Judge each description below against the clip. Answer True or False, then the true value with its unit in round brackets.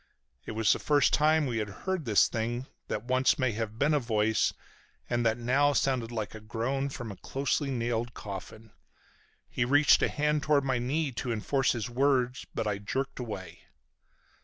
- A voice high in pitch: False (120 Hz)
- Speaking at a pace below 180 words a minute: False (185 wpm)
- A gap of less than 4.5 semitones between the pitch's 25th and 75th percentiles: True (3.7 semitones)